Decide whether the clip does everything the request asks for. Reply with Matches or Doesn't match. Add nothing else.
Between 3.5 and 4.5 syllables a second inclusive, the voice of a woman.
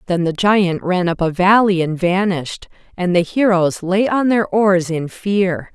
Matches